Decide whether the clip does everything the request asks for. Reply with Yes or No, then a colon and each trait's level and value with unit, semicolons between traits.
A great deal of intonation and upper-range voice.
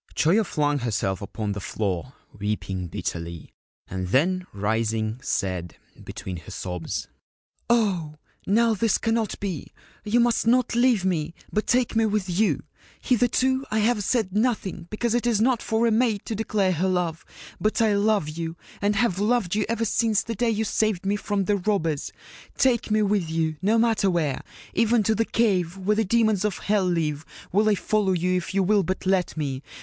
Yes: wide, 5.7 semitones; high, 200 Hz